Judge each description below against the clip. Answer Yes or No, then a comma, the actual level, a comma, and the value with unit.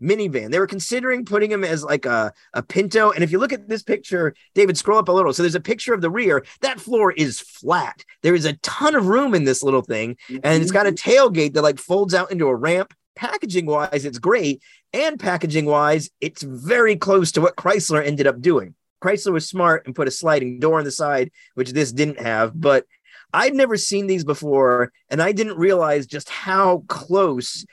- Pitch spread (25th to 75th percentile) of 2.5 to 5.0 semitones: No, wide, 5.4 semitones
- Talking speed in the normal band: No, fast, 215 wpm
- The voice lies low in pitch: No, medium, 180 Hz